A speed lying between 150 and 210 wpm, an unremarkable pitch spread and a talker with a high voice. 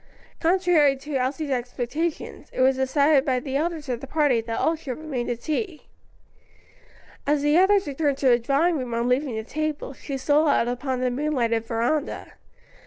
Yes: average, 175 wpm; average, 3.5 semitones; very high, 275 Hz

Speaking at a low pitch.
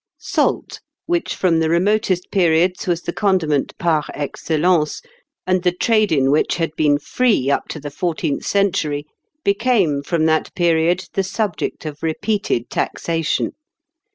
No: medium, 170 Hz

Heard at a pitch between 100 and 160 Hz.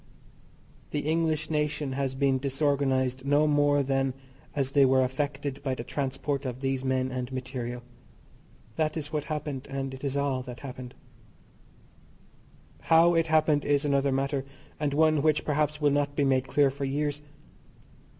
Yes: medium, 140 Hz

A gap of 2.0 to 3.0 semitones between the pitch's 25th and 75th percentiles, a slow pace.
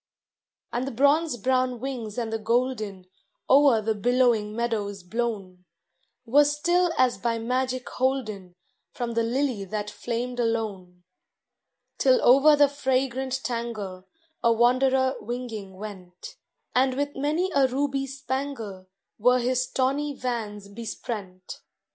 No: average, 3.7 semitones; slow, 125 wpm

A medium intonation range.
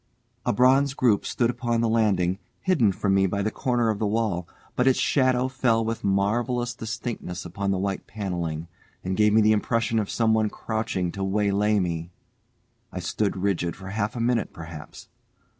Yes: average, 3.3 semitones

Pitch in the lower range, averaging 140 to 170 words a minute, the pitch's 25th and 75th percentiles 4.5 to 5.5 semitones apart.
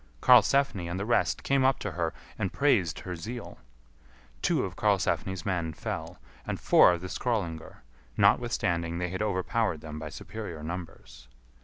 Yes: very low, 90 Hz; average, 155 wpm; average, 4.8 semitones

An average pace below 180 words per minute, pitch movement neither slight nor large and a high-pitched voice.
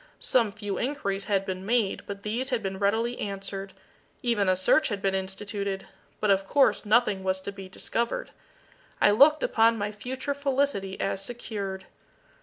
Yes: average, 165 wpm; average, 3.5 semitones; high, 205 Hz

